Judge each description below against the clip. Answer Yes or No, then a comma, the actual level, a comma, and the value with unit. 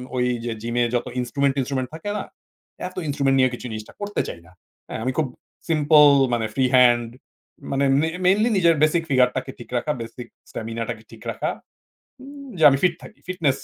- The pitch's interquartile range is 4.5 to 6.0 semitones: Yes, average, 5.0 semitones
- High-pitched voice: No, low, 135 Hz